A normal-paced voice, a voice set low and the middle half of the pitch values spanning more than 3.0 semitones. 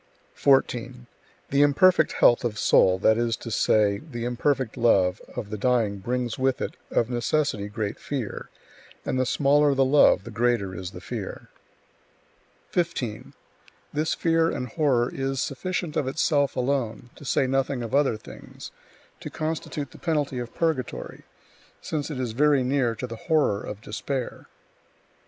Yes: average, 155 wpm; low, 125 Hz; average, 3.9 semitones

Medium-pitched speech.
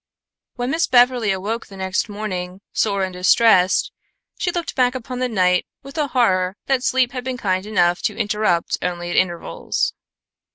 No: high, 210 Hz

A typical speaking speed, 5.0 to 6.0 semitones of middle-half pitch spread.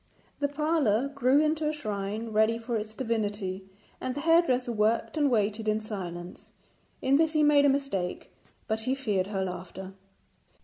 Yes: average, 165 wpm; wide, 5.5 semitones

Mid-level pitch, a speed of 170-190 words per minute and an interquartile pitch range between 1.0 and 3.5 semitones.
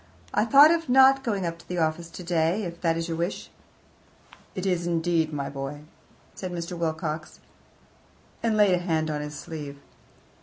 Yes: medium, 170 Hz; average, 175 wpm; average, 2.9 semitones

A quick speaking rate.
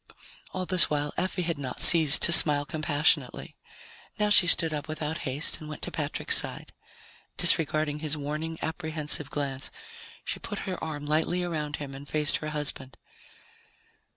No: average, 155 wpm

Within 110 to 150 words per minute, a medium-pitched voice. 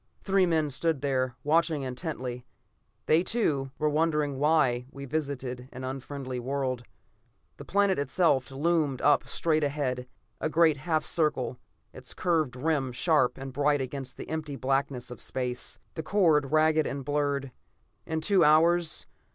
Yes: average, 145 wpm; medium, 145 Hz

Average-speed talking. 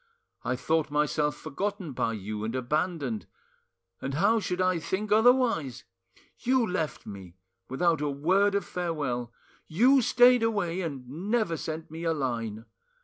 Yes: average, 145 wpm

